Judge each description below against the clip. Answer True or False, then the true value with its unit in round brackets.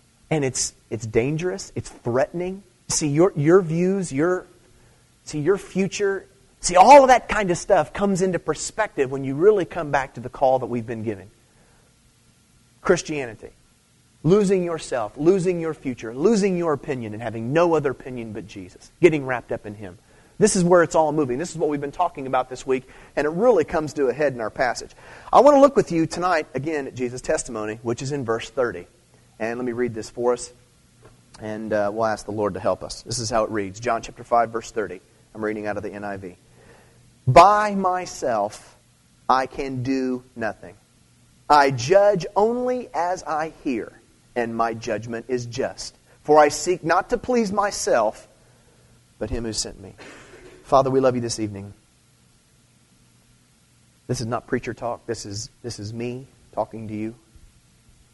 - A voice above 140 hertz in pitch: False (130 Hz)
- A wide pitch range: True (7.0 semitones)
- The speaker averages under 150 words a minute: False (185 wpm)